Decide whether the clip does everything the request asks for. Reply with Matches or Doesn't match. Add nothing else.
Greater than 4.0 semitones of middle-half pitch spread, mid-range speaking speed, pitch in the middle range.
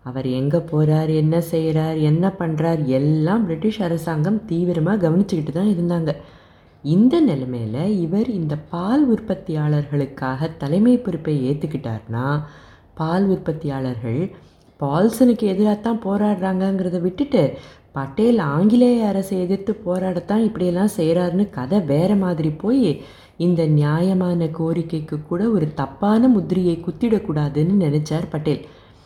Matches